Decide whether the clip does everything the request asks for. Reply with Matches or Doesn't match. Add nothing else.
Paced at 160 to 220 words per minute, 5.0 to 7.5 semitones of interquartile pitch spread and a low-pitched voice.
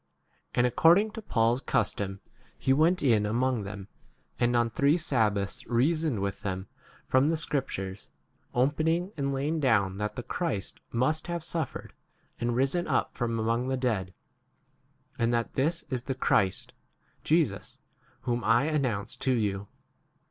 Doesn't match